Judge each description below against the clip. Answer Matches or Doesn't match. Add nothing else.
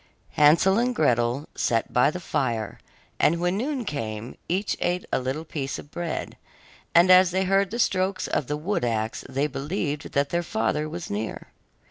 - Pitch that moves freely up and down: Matches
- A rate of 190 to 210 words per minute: Doesn't match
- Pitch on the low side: Doesn't match